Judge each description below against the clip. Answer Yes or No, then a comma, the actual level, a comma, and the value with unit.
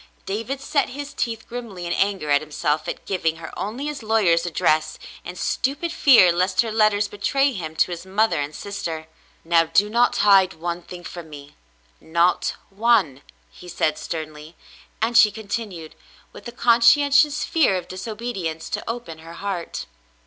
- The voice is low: No, high, 190 Hz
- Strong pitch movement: Yes, wide, 5.9 semitones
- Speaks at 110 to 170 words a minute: Yes, average, 165 wpm